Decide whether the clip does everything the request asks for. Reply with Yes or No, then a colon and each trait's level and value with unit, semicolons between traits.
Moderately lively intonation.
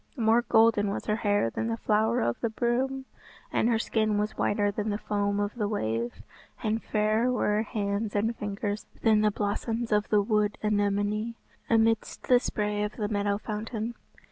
No: narrow, 1.6 semitones